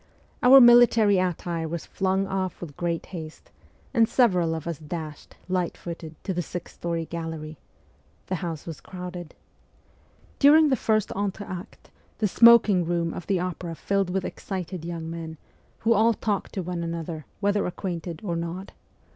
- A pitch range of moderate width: Yes, average, 3.1 semitones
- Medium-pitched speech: Yes, medium, 180 Hz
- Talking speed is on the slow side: No, average, 155 wpm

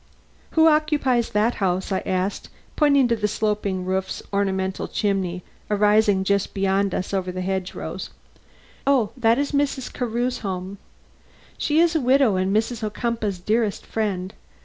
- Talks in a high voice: Yes, high, 210 Hz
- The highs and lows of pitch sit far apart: No, average, 4.2 semitones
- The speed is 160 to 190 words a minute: No, average, 150 wpm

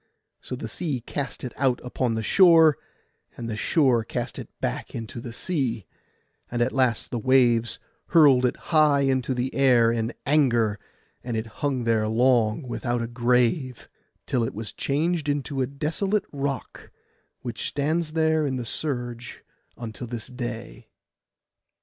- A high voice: No, low, 125 Hz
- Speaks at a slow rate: No, average, 155 wpm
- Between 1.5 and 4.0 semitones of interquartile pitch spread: Yes, average, 3.4 semitones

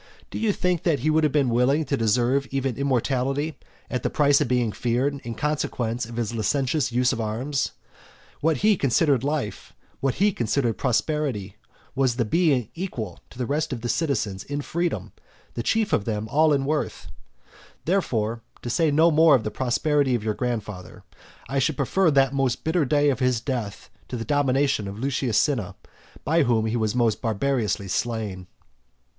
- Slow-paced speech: No, average, 180 wpm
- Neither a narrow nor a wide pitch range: Yes, average, 4.1 semitones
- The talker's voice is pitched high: No, low, 130 Hz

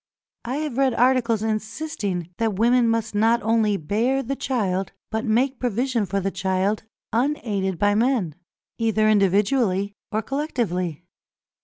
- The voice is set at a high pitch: Yes, high, 220 Hz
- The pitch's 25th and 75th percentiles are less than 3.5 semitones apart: No, average, 3.8 semitones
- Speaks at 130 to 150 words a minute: Yes, slow, 135 wpm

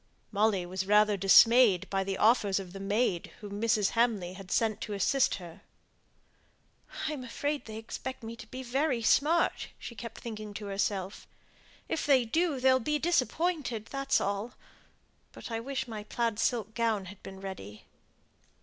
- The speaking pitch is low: No, high, 220 Hz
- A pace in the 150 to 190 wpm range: Yes, average, 165 wpm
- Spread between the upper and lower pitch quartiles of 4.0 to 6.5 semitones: Yes, average, 4.3 semitones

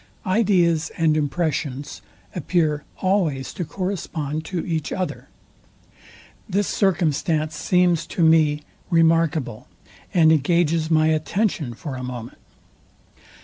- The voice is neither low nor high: Yes, medium, 160 Hz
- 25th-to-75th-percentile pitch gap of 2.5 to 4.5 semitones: Yes, average, 2.8 semitones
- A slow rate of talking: Yes, slow, 105 wpm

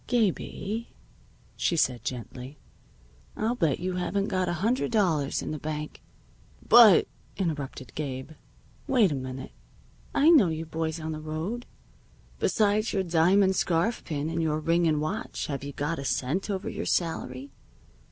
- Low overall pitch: No, medium, 165 Hz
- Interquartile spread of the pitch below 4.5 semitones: No, average, 5.0 semitones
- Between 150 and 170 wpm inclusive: Yes, average, 160 wpm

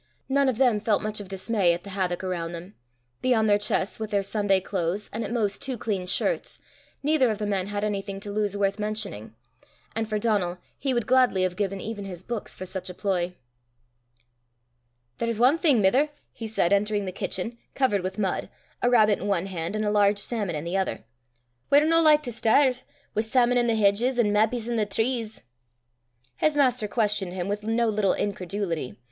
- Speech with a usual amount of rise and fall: Yes, average, 3.3 semitones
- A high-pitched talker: Yes, high, 210 Hz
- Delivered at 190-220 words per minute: Yes, average, 200 wpm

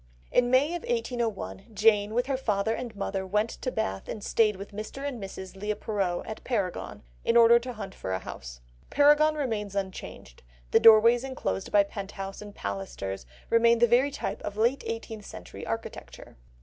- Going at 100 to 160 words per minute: No, average, 180 wpm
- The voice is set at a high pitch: Yes, high, 215 Hz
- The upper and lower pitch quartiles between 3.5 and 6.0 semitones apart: Yes, average, 3.8 semitones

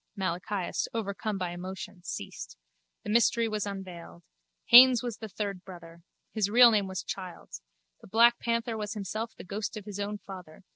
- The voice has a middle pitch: No, high, 205 Hz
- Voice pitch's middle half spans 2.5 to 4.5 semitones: Yes, average, 3.1 semitones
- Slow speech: No, average, 165 wpm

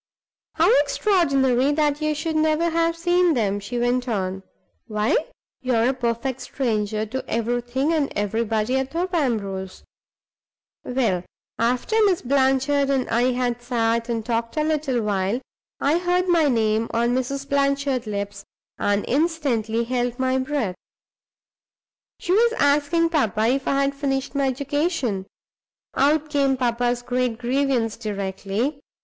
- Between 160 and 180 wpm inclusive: No, average, 140 wpm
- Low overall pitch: No, very high, 255 Hz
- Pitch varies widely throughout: No, average, 4.0 semitones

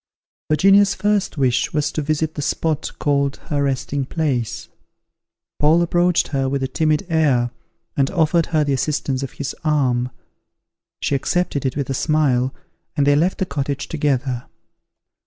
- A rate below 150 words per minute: No, average, 155 wpm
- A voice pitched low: No, medium, 145 Hz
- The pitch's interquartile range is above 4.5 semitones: No, average, 2.8 semitones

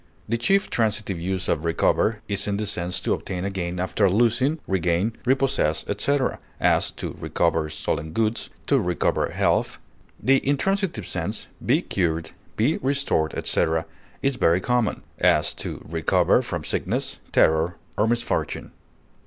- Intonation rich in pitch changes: Yes, wide, 6.1 semitones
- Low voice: Yes, low, 100 Hz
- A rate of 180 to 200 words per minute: No, average, 140 wpm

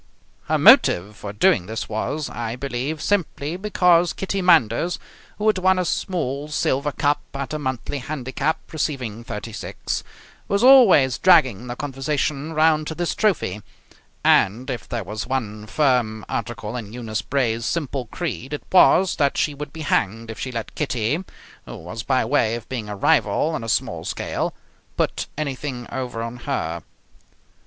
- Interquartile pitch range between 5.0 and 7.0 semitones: Yes, average, 5.3 semitones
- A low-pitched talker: Yes, low, 130 Hz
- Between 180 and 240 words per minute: No, average, 165 wpm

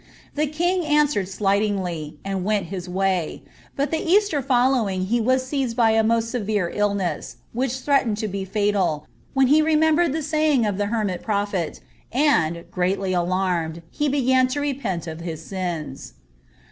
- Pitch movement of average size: No, wide, 6.6 semitones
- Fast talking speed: No, average, 160 wpm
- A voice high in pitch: Yes, high, 210 Hz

